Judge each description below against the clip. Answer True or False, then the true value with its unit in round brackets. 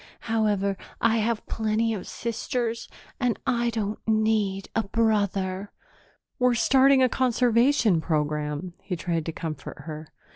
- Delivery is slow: True (125 wpm)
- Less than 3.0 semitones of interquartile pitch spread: False (3.9 semitones)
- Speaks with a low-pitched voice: False (215 Hz)